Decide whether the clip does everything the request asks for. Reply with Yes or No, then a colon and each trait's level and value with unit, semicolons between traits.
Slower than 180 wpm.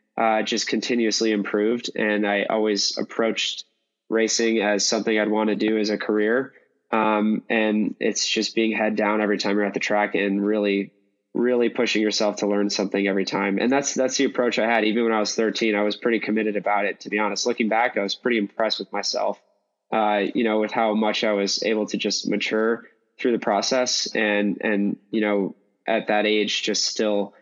No: fast, 205 wpm